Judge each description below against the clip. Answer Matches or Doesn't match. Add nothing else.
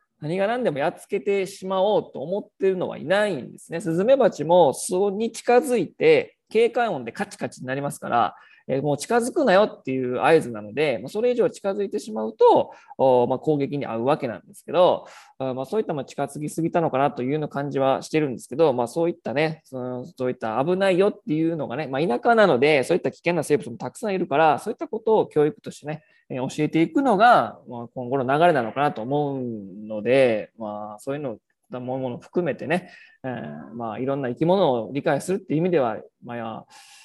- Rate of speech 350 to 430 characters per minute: Matches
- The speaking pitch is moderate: Matches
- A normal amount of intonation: Doesn't match